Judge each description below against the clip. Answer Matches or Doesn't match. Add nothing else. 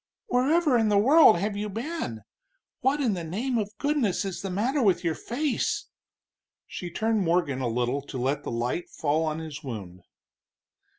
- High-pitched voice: Matches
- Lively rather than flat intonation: Matches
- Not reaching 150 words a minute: Doesn't match